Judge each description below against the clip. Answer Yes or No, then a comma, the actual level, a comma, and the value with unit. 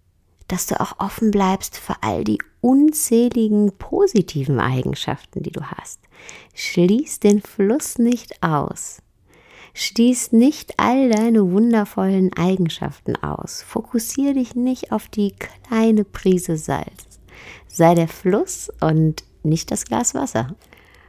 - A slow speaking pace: Yes, slow, 120 wpm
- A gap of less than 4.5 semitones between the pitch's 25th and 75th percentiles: No, average, 5.3 semitones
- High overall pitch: Yes, high, 205 Hz